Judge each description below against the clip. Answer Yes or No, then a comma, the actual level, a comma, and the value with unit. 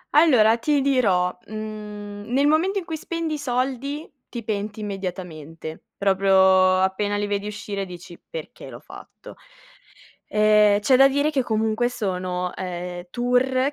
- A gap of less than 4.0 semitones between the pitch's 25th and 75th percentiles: No, wide, 5.7 semitones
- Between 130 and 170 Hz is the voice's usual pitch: No, high, 210 Hz